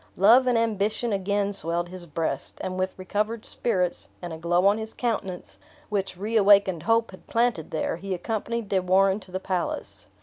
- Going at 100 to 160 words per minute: No, average, 175 wpm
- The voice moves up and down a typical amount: Yes, average, 3.3 semitones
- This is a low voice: No, high, 195 Hz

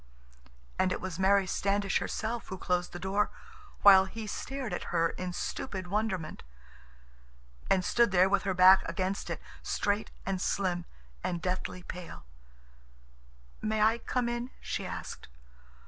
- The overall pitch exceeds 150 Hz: Yes, high, 190 Hz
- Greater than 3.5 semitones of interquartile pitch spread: No, narrow, 2.5 semitones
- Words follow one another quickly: No, average, 140 wpm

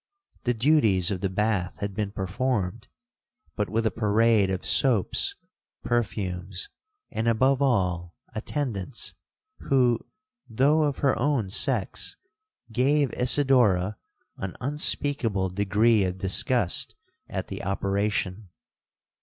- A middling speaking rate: No, slow, 110 wpm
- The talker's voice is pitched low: Yes, low, 110 Hz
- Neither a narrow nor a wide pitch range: Yes, average, 4.8 semitones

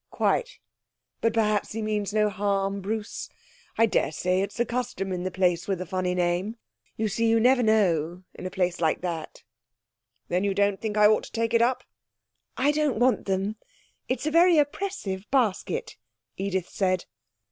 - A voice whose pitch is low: No, high, 205 Hz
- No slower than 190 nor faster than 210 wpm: No, average, 175 wpm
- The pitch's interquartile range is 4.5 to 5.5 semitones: No, average, 3.6 semitones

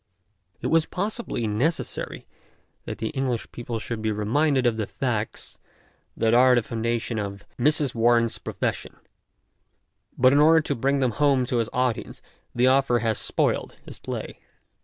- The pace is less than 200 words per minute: Yes, average, 165 wpm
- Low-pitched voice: Yes, low, 120 Hz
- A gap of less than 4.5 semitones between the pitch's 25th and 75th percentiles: Yes, average, 3.3 semitones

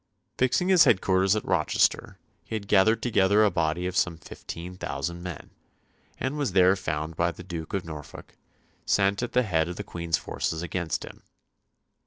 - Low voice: Yes, very low, 90 Hz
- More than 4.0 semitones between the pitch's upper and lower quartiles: No, average, 3.4 semitones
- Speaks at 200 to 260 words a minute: No, average, 175 wpm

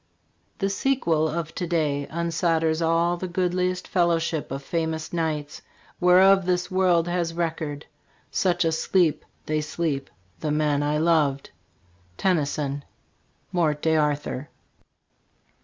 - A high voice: No, medium, 165 Hz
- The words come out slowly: Yes, slow, 130 wpm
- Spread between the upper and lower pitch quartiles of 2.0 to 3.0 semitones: Yes, average, 2.7 semitones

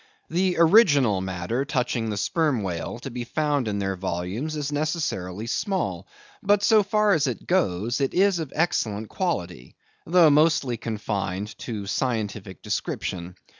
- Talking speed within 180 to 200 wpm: No, average, 145 wpm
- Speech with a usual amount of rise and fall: No, wide, 8.2 semitones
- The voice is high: No, low, 125 Hz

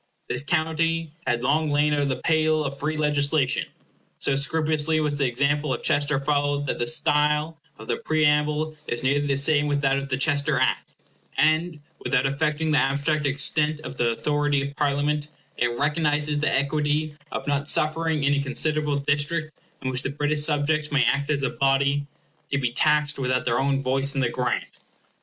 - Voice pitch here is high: No, medium, 145 Hz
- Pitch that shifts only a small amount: Yes, narrow, 1.8 semitones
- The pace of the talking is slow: No, average, 185 wpm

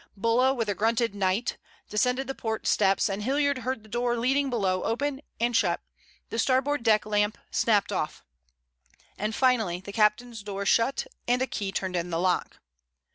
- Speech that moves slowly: No, average, 175 wpm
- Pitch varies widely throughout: No, average, 3.8 semitones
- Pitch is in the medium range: No, high, 225 Hz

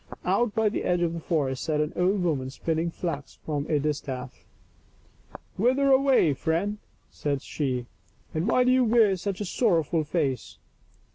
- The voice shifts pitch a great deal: Yes, wide, 6.1 semitones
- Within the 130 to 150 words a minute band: No, average, 185 wpm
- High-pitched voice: No, medium, 165 Hz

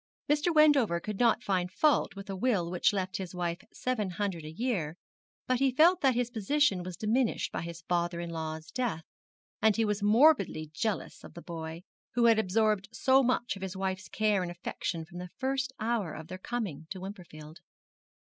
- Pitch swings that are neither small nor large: No, wide, 5.7 semitones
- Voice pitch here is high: Yes, high, 195 Hz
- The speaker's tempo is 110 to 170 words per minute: No, average, 195 wpm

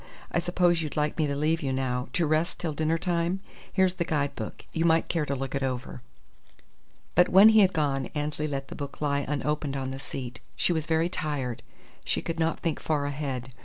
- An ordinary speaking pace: No, fast, 215 wpm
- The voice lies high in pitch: No, medium, 150 Hz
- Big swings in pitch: No, average, 3.3 semitones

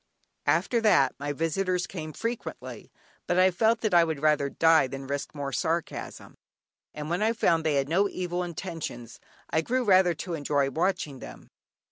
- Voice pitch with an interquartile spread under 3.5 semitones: No, average, 4.2 semitones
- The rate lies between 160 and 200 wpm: Yes, average, 170 wpm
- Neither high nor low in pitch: Yes, medium, 165 Hz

